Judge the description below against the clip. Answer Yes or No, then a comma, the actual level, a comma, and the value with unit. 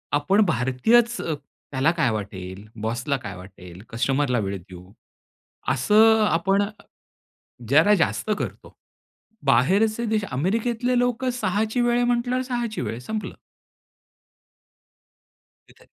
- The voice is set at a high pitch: No, medium, 165 Hz